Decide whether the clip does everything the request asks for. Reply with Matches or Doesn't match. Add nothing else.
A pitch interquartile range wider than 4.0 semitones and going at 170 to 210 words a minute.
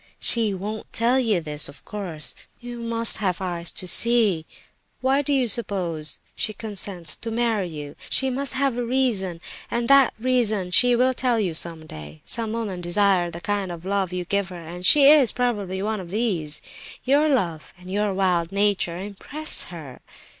Matches